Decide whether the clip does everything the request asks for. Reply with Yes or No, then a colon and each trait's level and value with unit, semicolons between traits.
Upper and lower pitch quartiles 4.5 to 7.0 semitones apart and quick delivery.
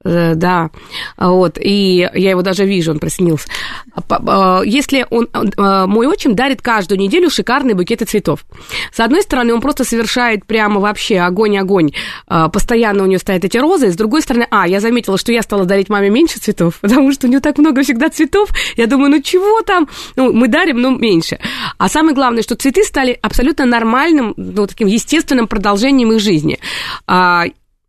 Yes: wide, 5.5 semitones; fast, 170 wpm